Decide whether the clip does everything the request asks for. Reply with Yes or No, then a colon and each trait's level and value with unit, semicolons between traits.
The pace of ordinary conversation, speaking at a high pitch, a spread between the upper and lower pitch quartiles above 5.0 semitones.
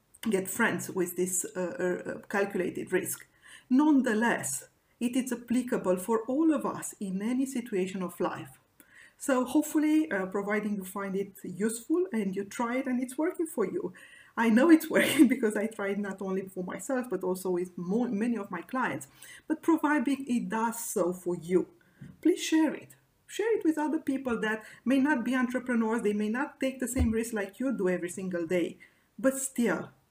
Yes: average, 185 wpm; high, 230 Hz; wide, 5.6 semitones